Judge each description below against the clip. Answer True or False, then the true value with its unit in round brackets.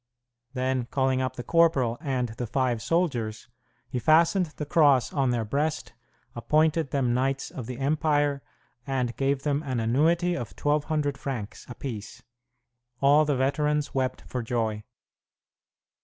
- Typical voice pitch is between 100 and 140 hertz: True (135 Hz)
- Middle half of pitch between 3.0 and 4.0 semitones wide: True (3.4 semitones)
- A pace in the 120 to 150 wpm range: True (140 wpm)